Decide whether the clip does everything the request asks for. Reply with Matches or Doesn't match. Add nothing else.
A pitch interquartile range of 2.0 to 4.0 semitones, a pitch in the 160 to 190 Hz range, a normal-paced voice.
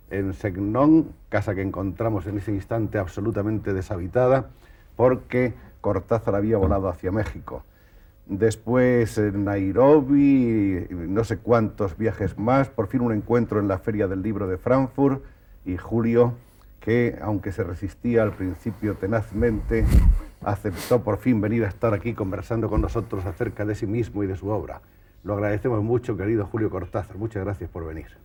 Doesn't match